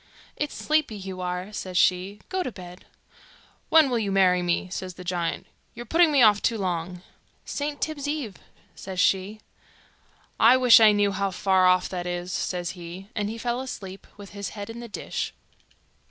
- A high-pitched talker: Yes, high, 200 Hz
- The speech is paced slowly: No, average, 185 wpm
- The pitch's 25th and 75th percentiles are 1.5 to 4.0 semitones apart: No, average, 4.5 semitones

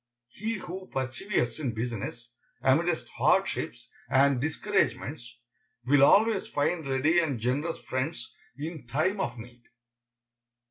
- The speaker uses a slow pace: Yes, slow, 110 wpm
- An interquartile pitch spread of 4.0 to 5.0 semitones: No, wide, 5.6 semitones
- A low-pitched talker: No, medium, 145 Hz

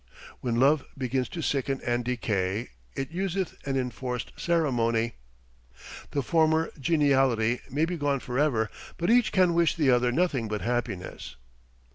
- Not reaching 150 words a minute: Yes, average, 140 wpm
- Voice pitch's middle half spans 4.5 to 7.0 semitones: Yes, average, 4.8 semitones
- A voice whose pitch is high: No, low, 135 Hz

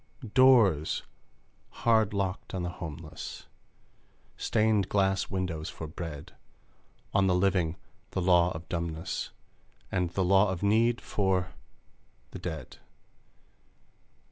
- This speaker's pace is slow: Yes, slow, 110 wpm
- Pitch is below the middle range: Yes, very low, 95 Hz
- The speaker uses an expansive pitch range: No, average, 2.7 semitones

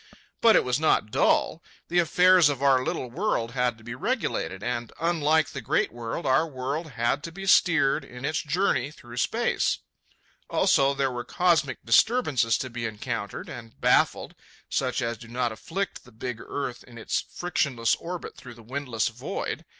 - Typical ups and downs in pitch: Yes, average, 5.0 semitones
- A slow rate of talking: No, average, 175 wpm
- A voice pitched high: No, low, 130 Hz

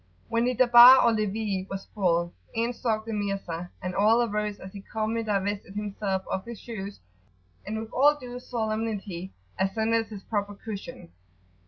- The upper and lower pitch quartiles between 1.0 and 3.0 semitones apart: Yes, narrow, 2.6 semitones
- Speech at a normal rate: Yes, average, 160 wpm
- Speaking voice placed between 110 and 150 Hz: No, high, 215 Hz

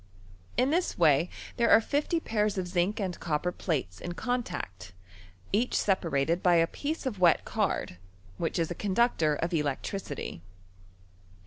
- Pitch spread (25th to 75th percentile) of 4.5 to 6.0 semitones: Yes, wide, 5.6 semitones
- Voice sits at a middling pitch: Yes, medium, 180 Hz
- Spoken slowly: No, average, 145 wpm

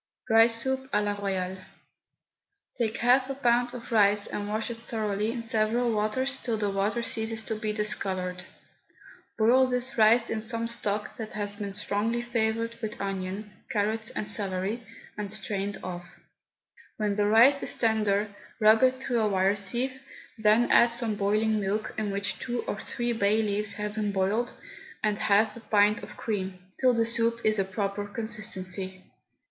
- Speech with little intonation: Yes, narrow, 2.3 semitones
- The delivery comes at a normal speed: Yes, average, 170 wpm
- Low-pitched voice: No, high, 215 Hz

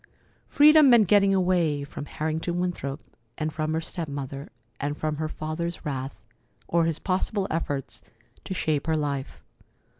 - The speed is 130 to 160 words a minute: Yes, average, 150 wpm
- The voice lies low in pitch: No, medium, 155 Hz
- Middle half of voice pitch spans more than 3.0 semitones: Yes, average, 3.7 semitones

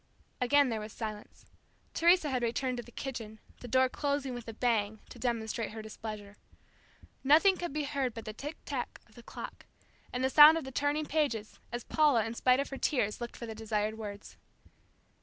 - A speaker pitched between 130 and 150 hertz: No, high, 245 Hz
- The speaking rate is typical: Yes, average, 195 wpm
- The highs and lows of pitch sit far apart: No, average, 4.3 semitones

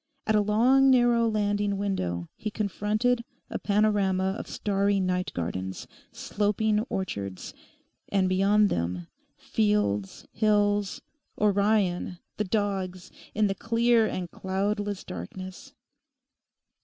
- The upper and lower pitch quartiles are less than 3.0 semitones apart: Yes, narrow, 2.4 semitones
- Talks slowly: Yes, slow, 105 wpm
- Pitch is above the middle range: Yes, high, 200 Hz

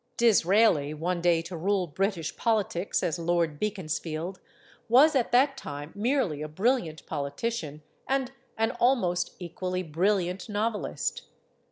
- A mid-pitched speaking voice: Yes, medium, 180 Hz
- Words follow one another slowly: Yes, slow, 130 wpm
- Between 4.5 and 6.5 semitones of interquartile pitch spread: Yes, wide, 5.5 semitones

